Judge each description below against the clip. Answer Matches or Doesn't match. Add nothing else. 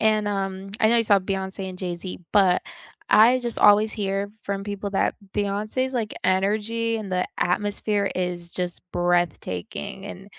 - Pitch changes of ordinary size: Doesn't match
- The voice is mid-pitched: Doesn't match